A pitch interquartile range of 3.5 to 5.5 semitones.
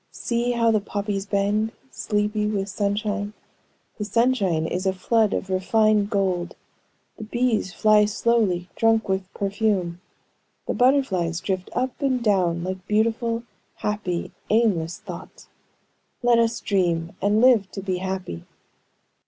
No: average, 3.1 semitones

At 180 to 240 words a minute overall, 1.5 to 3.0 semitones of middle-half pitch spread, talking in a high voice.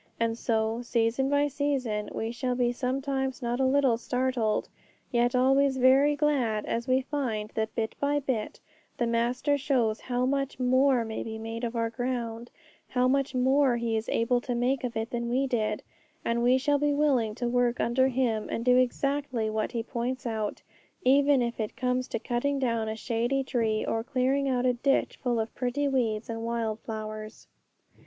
Yes: average, 185 wpm; average, 2.7 semitones; high, 245 Hz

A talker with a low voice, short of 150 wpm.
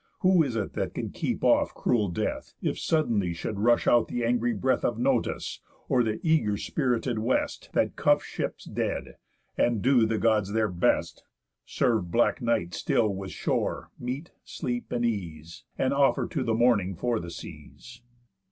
No: low, 115 Hz; average, 170 wpm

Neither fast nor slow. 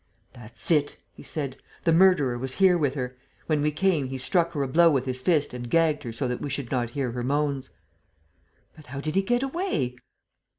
No: fast, 215 wpm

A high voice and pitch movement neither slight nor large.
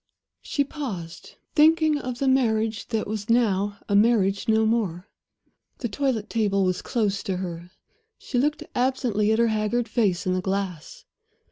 Yes: high, 220 Hz; average, 3.7 semitones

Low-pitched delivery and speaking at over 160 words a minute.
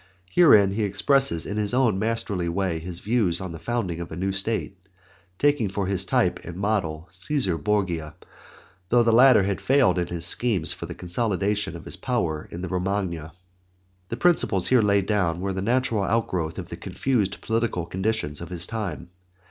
Yes: low, 100 Hz; average, 180 wpm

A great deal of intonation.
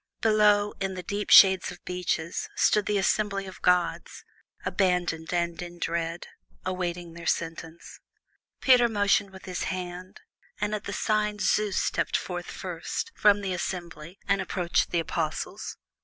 No: average, 2.9 semitones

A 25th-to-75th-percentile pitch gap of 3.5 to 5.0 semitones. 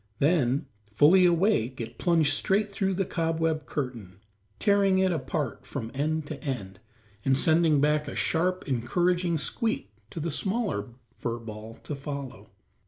No: wide, 5.4 semitones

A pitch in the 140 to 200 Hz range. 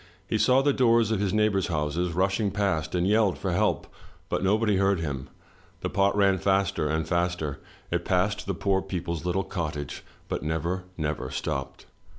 No: very low, 95 Hz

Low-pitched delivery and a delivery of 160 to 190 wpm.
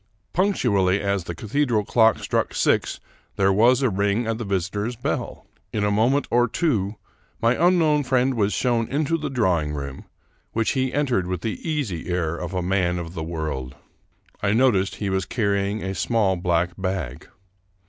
Yes: low, 100 Hz; average, 175 wpm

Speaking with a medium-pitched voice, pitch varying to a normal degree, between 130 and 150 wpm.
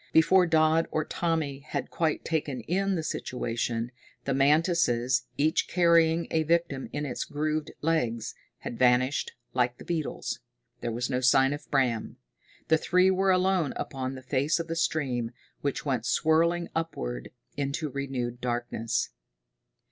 Yes: medium, 145 Hz; average, 4.7 semitones; average, 145 wpm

